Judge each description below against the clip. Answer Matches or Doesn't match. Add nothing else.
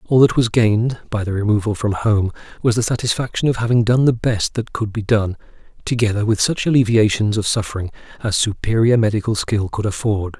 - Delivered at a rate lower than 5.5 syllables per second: Doesn't match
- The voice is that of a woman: Doesn't match